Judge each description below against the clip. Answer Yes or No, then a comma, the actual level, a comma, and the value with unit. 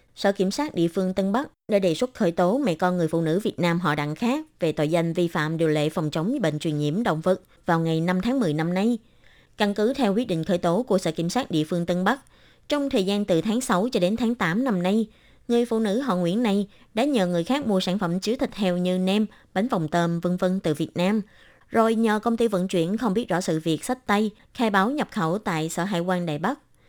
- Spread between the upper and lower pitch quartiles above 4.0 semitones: Yes, average, 4.9 semitones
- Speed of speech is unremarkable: No, fast, 265 wpm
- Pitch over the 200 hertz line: No, medium, 185 Hz